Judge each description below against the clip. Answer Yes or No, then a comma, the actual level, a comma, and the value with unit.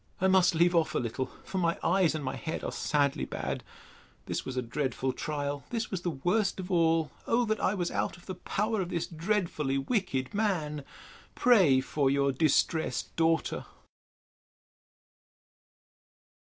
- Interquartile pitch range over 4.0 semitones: Yes, average, 5.0 semitones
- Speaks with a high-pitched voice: No, medium, 165 Hz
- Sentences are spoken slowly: No, average, 155 wpm